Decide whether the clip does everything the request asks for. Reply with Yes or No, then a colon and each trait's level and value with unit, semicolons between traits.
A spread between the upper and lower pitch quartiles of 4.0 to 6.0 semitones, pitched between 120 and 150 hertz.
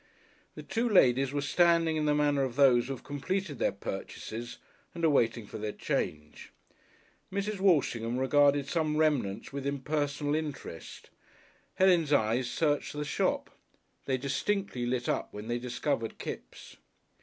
Yes: average, 4.3 semitones; medium, 140 Hz